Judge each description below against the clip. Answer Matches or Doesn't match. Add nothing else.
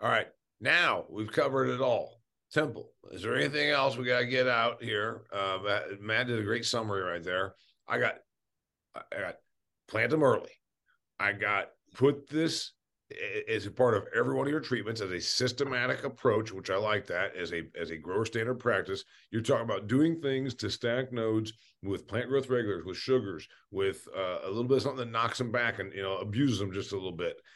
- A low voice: Matches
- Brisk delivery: Matches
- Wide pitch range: Doesn't match